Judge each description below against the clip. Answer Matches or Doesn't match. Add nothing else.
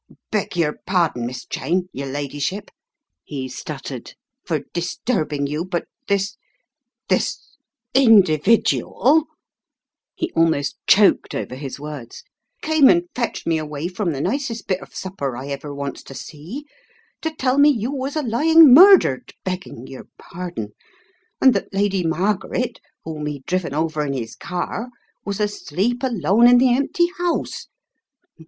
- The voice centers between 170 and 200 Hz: Matches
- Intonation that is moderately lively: Doesn't match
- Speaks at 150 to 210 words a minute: Matches